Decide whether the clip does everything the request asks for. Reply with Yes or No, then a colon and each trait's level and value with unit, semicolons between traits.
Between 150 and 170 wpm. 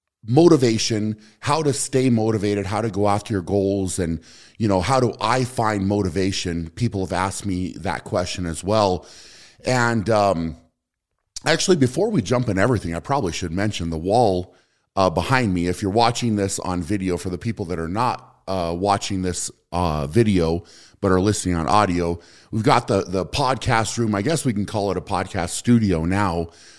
No: average, 185 wpm